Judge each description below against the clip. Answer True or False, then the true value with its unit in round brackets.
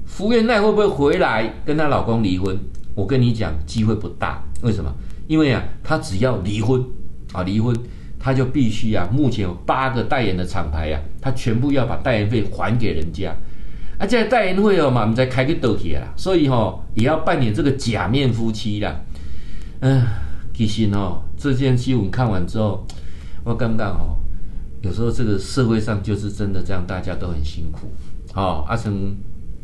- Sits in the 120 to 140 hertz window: False (110 Hz)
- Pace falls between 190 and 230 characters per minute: False (275 characters per minute)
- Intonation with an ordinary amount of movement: False (6.4 semitones)